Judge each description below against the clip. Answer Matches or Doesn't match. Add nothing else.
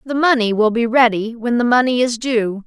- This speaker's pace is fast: Matches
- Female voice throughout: Matches